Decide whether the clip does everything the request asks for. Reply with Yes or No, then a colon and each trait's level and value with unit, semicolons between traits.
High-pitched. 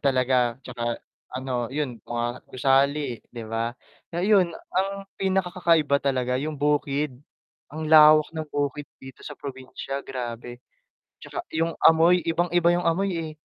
No: medium, 145 Hz